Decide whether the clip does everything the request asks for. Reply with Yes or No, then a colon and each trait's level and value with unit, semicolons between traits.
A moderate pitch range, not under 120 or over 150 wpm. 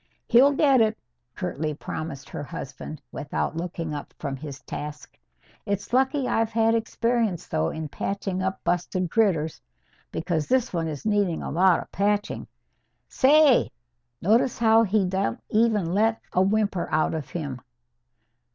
No: wide, 6.0 semitones; average, 145 wpm